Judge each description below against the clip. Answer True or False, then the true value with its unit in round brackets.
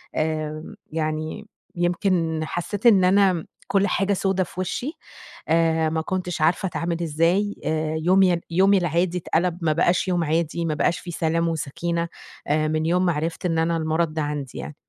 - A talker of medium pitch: True (170 Hz)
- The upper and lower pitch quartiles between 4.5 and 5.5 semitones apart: False (2.4 semitones)